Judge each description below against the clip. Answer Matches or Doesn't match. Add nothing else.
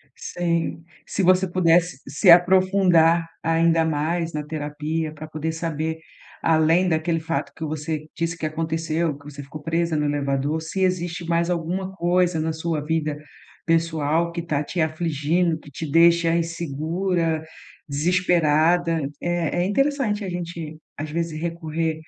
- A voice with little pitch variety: Matches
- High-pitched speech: Doesn't match